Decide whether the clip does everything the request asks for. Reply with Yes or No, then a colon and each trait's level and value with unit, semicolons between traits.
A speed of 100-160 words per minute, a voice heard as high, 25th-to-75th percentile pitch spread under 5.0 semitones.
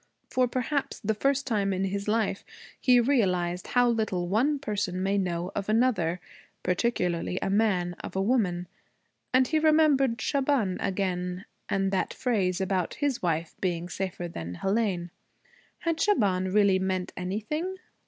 No: average, 145 wpm; high, 200 Hz; average, 5.3 semitones